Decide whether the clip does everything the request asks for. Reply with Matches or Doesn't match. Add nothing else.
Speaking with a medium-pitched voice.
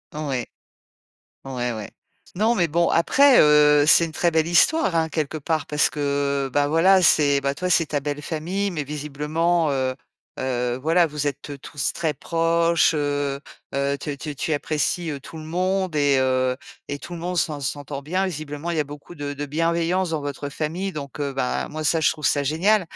Matches